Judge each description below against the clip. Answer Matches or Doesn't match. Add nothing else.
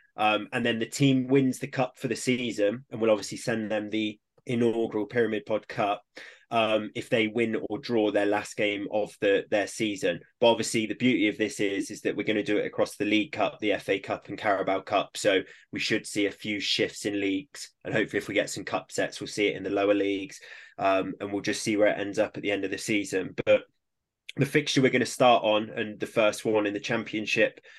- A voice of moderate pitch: Doesn't match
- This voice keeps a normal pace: Doesn't match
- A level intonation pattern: Matches